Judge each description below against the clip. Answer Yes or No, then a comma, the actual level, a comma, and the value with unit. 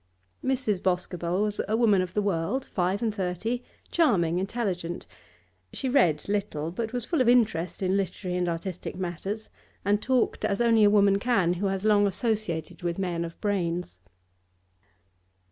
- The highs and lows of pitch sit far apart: No, average, 3.7 semitones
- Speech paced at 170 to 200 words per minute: No, average, 160 wpm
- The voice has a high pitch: Yes, high, 195 Hz